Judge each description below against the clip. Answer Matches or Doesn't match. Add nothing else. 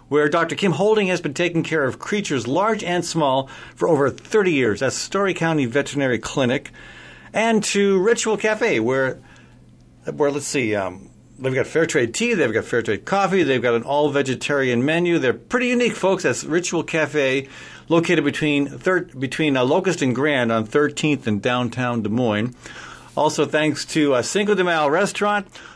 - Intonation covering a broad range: Matches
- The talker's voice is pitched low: Doesn't match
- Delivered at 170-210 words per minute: Matches